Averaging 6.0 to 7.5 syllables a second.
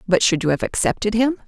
Yes: 6.5 syllables/s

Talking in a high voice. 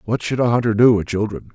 No: low, 110 Hz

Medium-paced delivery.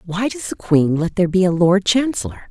No: fast, 240 wpm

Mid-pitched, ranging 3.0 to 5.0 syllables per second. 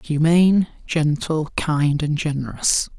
Yes: medium, 155 Hz; 3.8 syllables/s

